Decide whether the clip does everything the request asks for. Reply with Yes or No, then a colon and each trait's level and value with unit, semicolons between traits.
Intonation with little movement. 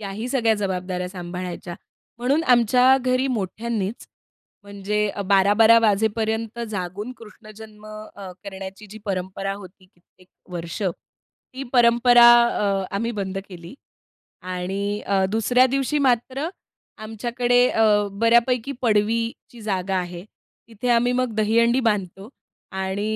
No: average, 3.6 semitones